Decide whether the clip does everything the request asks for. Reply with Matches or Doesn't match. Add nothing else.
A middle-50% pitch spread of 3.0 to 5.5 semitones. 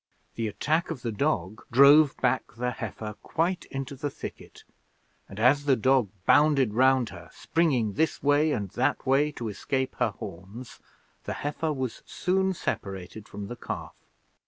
Matches